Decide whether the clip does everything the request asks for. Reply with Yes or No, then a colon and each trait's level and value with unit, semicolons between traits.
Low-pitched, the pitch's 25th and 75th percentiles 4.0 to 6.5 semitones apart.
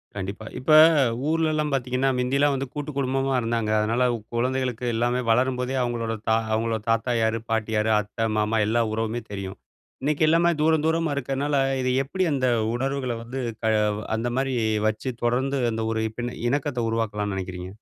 No: low, 125 Hz; average, 3.3 semitones